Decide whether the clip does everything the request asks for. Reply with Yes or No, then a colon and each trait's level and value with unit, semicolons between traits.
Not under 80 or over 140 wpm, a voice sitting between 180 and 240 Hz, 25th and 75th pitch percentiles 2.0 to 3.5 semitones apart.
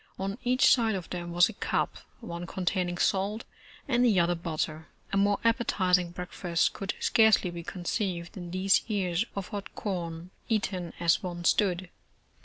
No: average, 160 wpm; medium, 185 Hz; average, 2.9 semitones